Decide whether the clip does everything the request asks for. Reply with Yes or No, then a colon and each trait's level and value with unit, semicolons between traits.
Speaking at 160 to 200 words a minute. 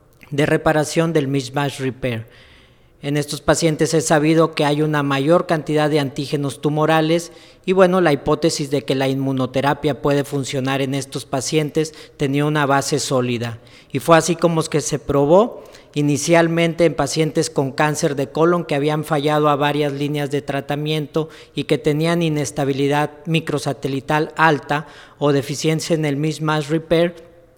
No: average, 150 wpm